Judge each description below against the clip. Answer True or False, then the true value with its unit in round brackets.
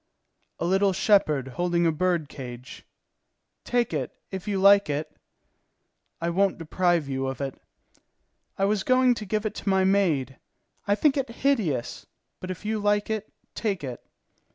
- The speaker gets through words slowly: False (160 wpm)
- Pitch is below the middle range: False (190 Hz)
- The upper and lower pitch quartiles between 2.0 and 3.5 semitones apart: False (5.3 semitones)